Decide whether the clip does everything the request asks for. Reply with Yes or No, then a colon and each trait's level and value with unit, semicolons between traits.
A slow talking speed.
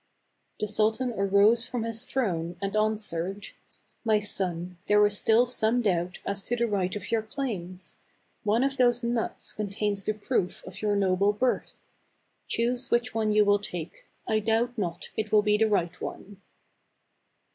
No: average, 170 wpm